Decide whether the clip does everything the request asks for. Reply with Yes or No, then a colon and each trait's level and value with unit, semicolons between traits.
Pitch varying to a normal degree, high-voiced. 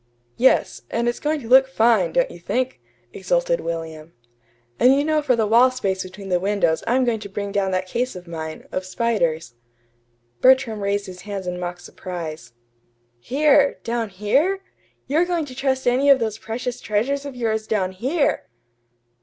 No: wide, 6.0 semitones; high, 225 Hz